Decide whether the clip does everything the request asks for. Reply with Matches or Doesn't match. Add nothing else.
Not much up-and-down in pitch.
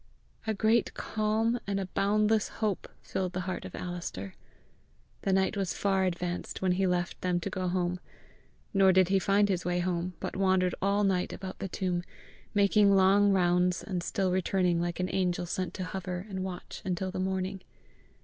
Matches